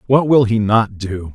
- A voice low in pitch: Yes, low, 110 Hz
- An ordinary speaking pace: No, fast, 225 wpm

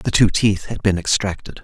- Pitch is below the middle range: Yes, very low, 95 Hz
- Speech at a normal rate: No, fast, 220 wpm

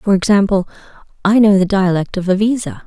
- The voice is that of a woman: Yes, female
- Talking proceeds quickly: No, average, 170 wpm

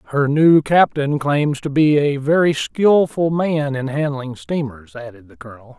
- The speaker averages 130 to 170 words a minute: Yes, average, 165 wpm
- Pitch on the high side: No, medium, 145 Hz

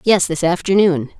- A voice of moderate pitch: Yes, medium, 175 Hz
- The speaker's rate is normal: Yes, average, 150 wpm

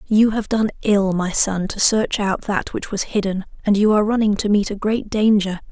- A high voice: Yes, high, 205 Hz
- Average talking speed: No, fast, 230 wpm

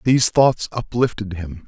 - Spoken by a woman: No, male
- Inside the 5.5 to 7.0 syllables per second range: No, 4.6 syllables/s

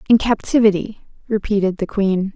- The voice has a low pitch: No, high, 205 Hz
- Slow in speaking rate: Yes, slow, 125 wpm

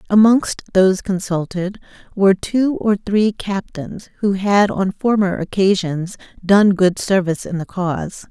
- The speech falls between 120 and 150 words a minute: Yes, slow, 135 wpm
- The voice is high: Yes, high, 195 Hz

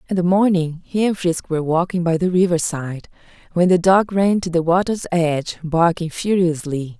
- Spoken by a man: No, female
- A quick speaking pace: No, average, 180 wpm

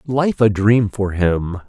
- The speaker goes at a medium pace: Yes, average, 180 wpm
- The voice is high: No, low, 105 Hz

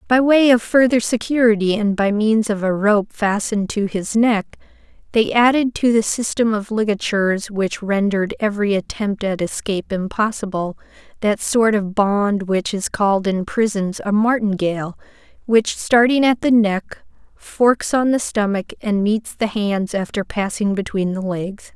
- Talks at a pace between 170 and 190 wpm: No, average, 160 wpm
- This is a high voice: Yes, high, 210 Hz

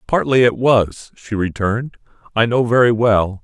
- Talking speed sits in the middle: Yes, average, 155 wpm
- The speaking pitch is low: Yes, low, 110 Hz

